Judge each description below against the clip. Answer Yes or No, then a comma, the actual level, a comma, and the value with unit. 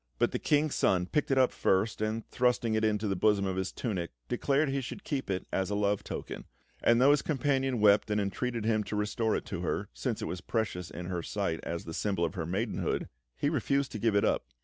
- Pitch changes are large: No, average, 4.7 semitones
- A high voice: No, low, 105 Hz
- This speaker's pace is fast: Yes, fast, 240 wpm